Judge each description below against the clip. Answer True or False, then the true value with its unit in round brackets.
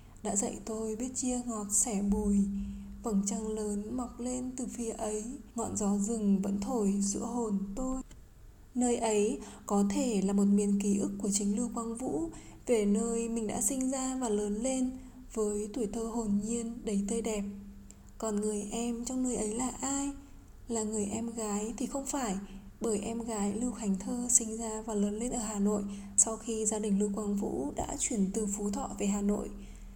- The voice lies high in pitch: True (220 Hz)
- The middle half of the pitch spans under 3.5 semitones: True (2.6 semitones)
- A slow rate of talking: False (200 wpm)